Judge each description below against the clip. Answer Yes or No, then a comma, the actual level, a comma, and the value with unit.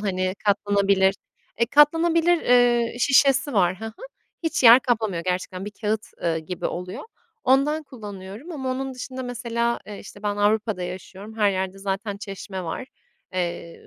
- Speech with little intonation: No, average, 4.8 semitones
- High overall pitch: Yes, high, 210 Hz